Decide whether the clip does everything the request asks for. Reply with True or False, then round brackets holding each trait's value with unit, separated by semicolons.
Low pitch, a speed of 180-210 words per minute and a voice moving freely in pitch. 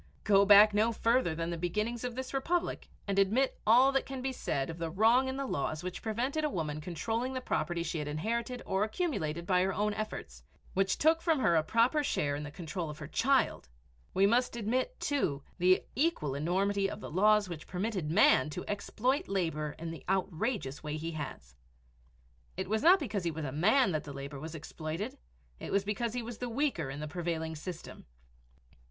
False (195 Hz; 205 wpm; 6.9 semitones)